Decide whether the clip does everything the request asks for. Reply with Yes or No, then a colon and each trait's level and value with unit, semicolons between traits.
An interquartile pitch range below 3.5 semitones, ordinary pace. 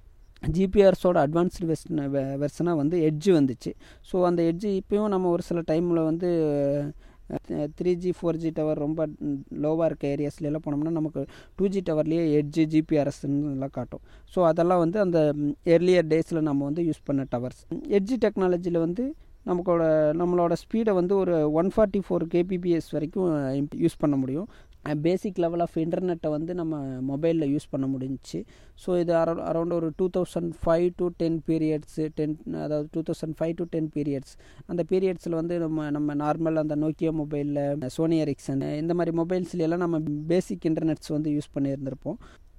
No: average, 2.8 semitones; fast, 155 wpm